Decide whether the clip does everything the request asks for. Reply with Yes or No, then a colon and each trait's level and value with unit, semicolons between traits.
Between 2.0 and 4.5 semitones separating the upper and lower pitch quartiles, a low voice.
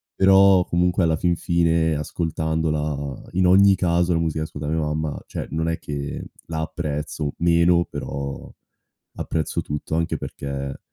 Yes: narrow, 2.4 semitones; very low, 80 Hz